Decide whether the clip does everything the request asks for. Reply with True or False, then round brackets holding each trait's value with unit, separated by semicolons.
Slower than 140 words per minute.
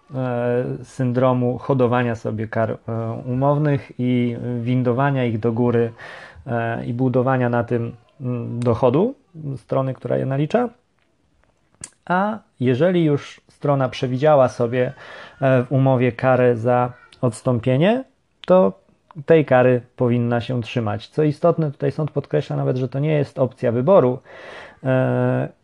True (125 wpm)